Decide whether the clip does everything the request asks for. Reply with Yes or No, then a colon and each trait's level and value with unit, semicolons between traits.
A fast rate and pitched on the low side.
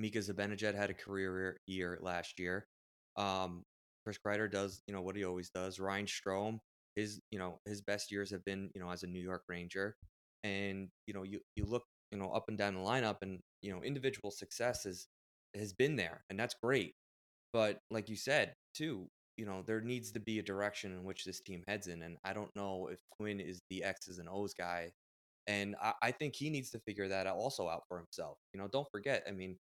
Yes: fast, 220 wpm; very low, 95 Hz